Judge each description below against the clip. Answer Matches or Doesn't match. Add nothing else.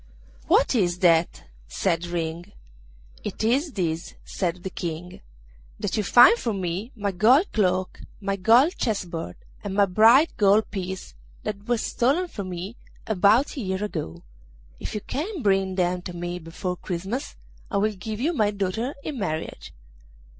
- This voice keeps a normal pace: Matches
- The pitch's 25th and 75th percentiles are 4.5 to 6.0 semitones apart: Doesn't match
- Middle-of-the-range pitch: Doesn't match